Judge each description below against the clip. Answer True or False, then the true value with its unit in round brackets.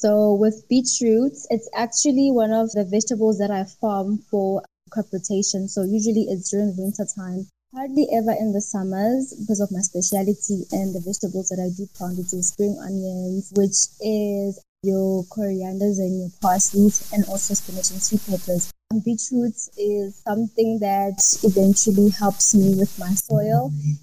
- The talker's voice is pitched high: True (200 Hz)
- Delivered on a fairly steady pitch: True (2.1 semitones)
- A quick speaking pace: False (160 wpm)